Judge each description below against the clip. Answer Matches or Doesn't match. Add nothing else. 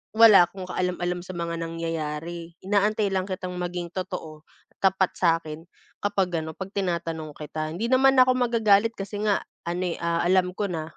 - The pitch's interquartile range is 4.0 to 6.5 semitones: Doesn't match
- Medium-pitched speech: Matches